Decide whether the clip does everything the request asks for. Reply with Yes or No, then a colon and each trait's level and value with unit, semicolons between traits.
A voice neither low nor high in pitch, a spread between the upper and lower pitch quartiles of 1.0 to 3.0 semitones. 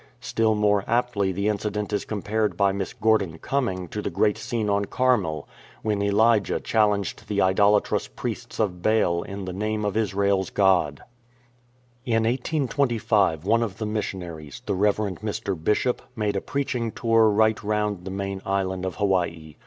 No: low, 105 Hz; narrow, 2.4 semitones